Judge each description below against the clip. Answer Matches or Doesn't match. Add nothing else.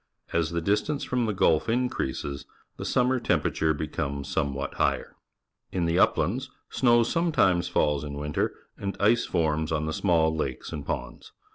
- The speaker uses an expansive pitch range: Matches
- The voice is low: Matches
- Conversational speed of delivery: Matches